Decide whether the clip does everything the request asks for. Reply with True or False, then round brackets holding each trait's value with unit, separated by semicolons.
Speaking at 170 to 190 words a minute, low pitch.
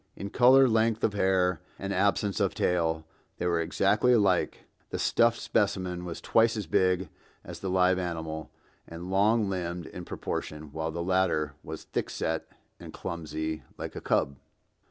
False (160 wpm; 90 Hz)